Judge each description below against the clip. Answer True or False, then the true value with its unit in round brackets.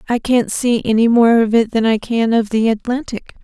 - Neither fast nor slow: False (225 wpm)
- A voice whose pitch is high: True (230 Hz)